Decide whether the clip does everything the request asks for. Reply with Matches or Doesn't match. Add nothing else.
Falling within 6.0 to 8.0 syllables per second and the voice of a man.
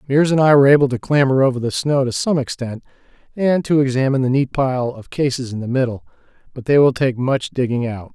Matches